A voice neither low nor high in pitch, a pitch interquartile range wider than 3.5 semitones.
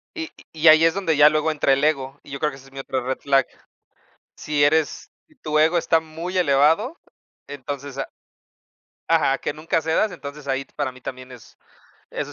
No: medium, 150 Hz; average, 2.9 semitones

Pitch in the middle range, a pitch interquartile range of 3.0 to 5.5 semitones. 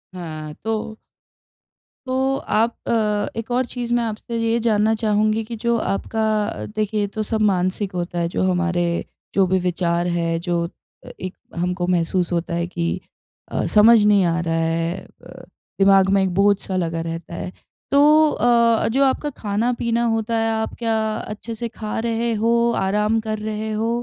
No: high, 210 Hz; average, 4.1 semitones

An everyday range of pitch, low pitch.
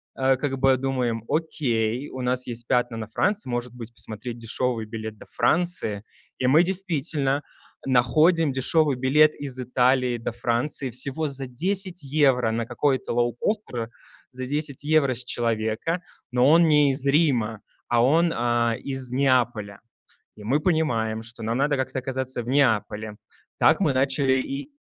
Yes: average, 3.5 semitones; low, 130 Hz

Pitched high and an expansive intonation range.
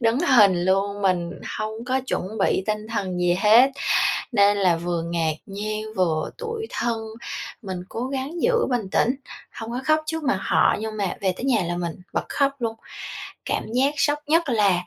Yes: high, 215 Hz; wide, 5.7 semitones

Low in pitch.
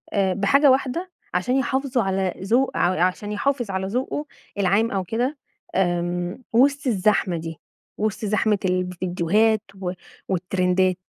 No: high, 200 Hz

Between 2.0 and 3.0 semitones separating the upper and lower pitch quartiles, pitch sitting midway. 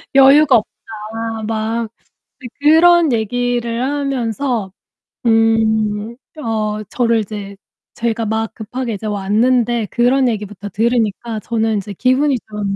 No: narrow, 2.4 semitones; high, 225 Hz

